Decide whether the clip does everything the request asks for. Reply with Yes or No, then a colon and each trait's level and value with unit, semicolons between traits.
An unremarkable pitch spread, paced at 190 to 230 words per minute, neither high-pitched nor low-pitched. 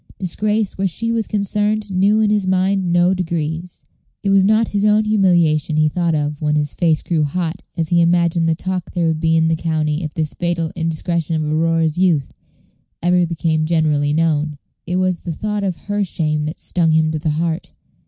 Yes: average, 3.0 semitones; average, 200 wpm; medium, 170 Hz